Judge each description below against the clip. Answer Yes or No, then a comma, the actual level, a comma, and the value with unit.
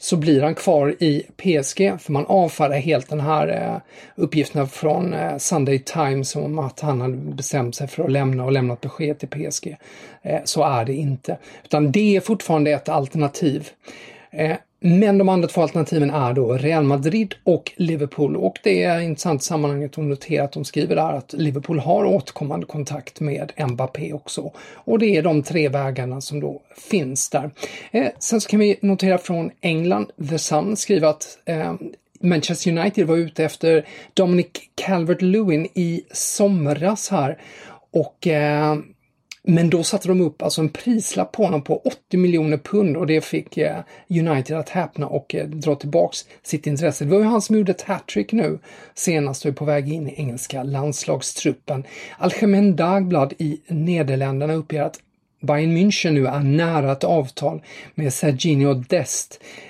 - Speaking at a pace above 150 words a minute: Yes, average, 165 wpm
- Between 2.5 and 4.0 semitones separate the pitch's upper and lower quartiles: Yes, average, 3.5 semitones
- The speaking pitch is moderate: Yes, medium, 155 Hz